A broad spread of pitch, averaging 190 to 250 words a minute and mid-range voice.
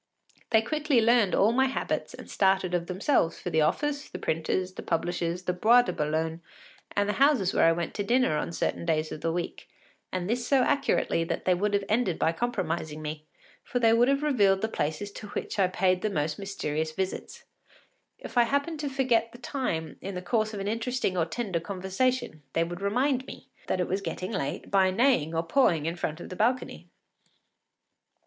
No: wide, 6.3 semitones; average, 200 wpm; high, 195 Hz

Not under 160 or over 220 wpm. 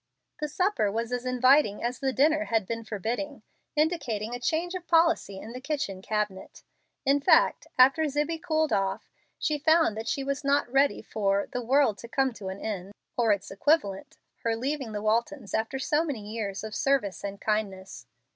Yes: average, 185 wpm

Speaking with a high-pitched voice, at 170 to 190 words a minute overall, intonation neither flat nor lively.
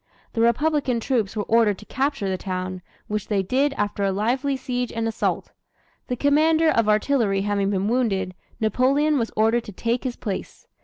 Yes: high, 230 Hz; average, 175 wpm; average, 4.4 semitones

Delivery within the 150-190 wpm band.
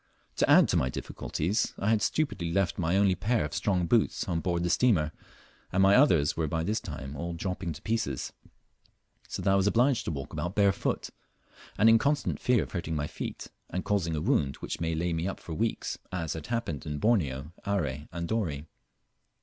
No: fast, 205 wpm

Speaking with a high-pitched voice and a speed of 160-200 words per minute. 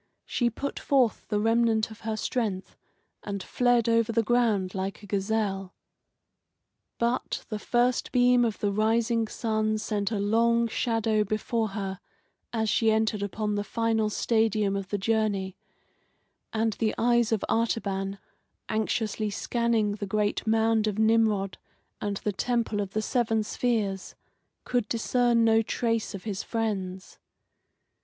No: high, 220 Hz; average, 140 wpm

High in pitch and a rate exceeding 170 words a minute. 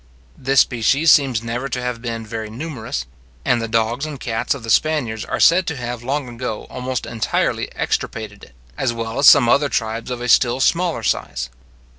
No: low, 120 Hz; average, 190 wpm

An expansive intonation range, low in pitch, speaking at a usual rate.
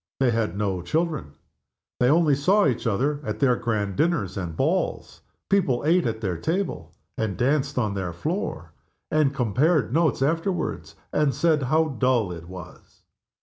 Yes: wide, 7.2 semitones; low, 130 Hz; average, 155 wpm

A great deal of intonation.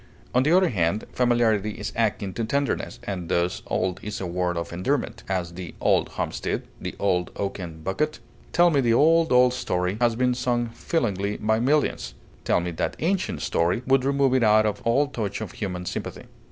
Yes: wide, 5.8 semitones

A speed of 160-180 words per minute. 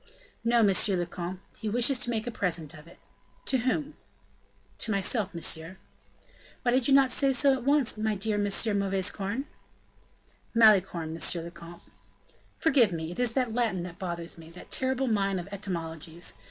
Yes: average, 170 wpm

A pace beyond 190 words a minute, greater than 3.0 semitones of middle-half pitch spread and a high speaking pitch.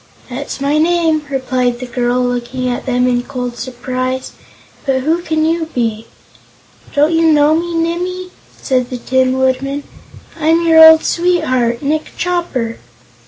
No: average, 145 wpm; average, 4.3 semitones; very high, 275 Hz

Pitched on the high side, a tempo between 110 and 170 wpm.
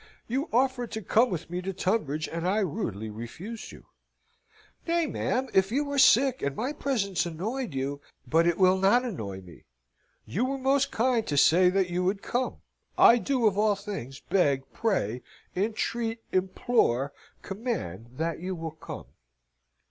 Yes: high, 195 Hz; average, 165 wpm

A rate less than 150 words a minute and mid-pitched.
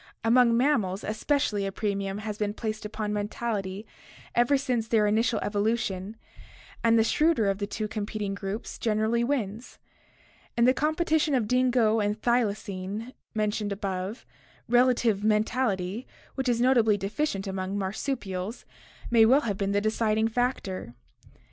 No: slow, 135 wpm; high, 215 Hz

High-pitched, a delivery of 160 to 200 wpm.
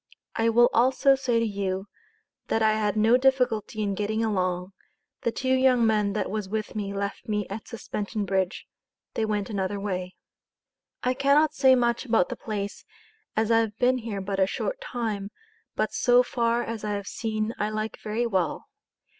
Yes: high, 215 Hz; average, 180 wpm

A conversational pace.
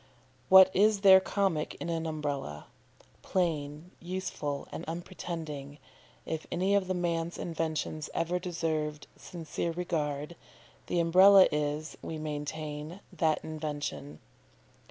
No: slow, 110 wpm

